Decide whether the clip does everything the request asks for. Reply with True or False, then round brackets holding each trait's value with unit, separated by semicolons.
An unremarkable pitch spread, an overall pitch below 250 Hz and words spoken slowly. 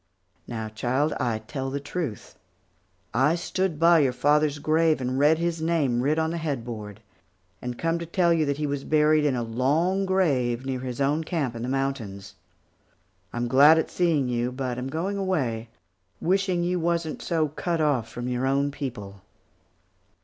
False (4.7 semitones; 140 Hz; 175 wpm)